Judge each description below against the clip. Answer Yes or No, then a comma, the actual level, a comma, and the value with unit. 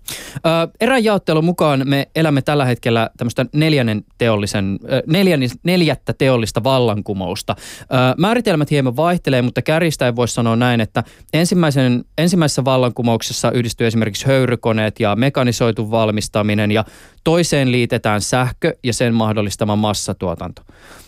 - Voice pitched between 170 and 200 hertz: No, low, 125 Hz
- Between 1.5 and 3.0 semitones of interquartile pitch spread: No, average, 4.9 semitones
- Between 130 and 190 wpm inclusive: No, average, 105 wpm